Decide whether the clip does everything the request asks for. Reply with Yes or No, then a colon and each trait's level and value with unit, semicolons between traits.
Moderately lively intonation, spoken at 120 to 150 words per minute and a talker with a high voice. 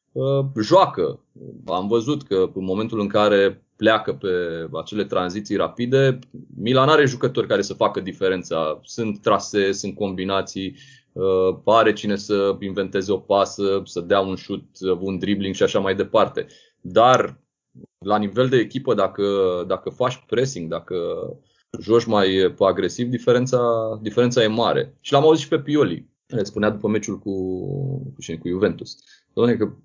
No: average, 4.2 semitones; average, 145 wpm; low, 105 Hz